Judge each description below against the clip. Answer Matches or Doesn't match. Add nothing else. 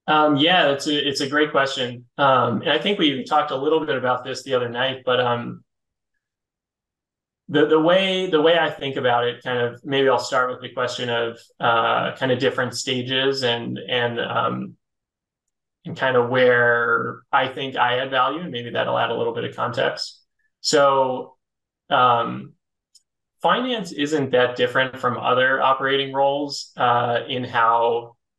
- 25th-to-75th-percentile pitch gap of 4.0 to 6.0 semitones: Doesn't match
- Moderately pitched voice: Doesn't match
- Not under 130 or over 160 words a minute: Doesn't match